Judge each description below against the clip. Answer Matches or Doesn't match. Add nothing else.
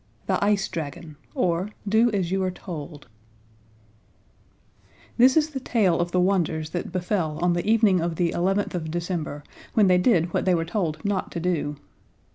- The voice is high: Doesn't match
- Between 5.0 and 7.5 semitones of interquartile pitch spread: Doesn't match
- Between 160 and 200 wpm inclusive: Matches